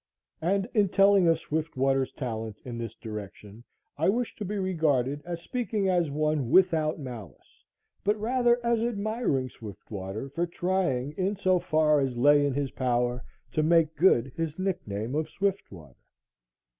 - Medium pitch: Yes, medium, 155 Hz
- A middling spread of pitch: No, wide, 6.9 semitones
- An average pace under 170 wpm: Yes, average, 150 wpm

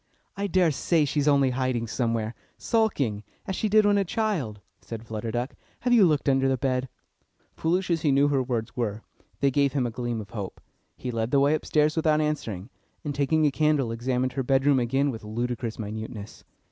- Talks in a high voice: No, low, 135 Hz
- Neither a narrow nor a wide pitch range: Yes, average, 4.6 semitones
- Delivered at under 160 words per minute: No, average, 195 wpm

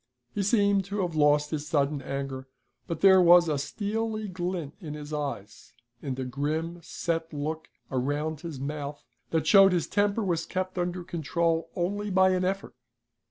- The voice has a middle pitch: Yes, medium, 165 Hz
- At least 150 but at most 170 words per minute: Yes, average, 165 wpm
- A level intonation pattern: No, average, 4.2 semitones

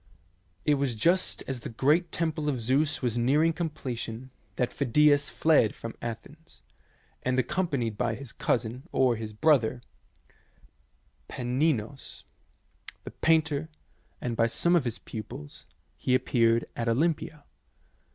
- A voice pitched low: Yes, low, 130 Hz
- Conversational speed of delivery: No, slow, 130 wpm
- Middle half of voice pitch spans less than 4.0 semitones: No, average, 4.6 semitones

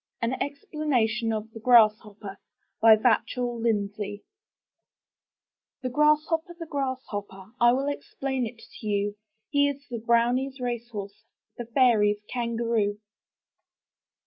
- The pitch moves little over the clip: No, average, 3.5 semitones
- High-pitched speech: Yes, high, 235 Hz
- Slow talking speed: Yes, slow, 105 wpm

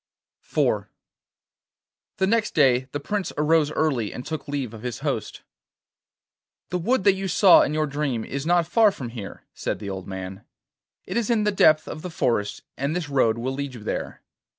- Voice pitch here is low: No, medium, 145 Hz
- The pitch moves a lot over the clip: Yes, wide, 6.6 semitones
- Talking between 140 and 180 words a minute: No, average, 190 wpm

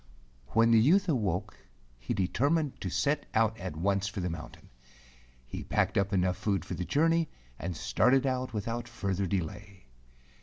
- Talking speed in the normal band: Yes, average, 160 wpm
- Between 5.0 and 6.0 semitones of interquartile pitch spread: Yes, wide, 5.5 semitones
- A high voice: No, low, 105 Hz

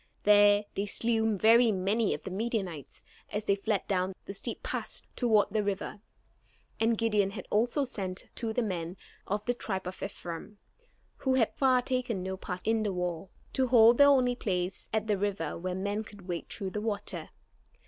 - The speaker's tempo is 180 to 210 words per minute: Yes, average, 190 wpm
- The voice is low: No, high, 205 Hz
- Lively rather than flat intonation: No, average, 3.1 semitones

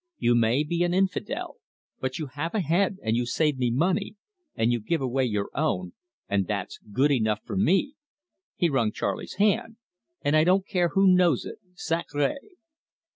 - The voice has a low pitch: No, medium, 150 Hz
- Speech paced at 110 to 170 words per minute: No, average, 180 wpm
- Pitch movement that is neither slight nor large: No, wide, 7.1 semitones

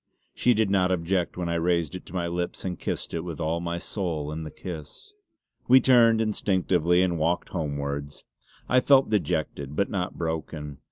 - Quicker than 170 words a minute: Yes, average, 180 wpm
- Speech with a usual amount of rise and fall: Yes, average, 3.3 semitones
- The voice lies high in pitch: No, very low, 85 Hz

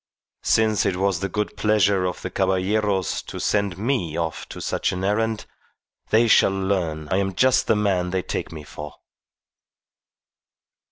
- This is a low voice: Yes, very low, 95 Hz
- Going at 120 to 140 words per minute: No, average, 160 wpm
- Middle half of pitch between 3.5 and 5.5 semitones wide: No, narrow, 2.6 semitones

